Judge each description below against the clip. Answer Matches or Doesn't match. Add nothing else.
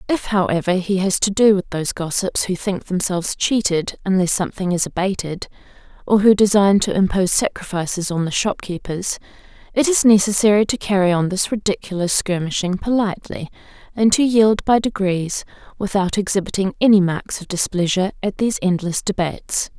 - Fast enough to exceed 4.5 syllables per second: Matches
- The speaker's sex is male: Doesn't match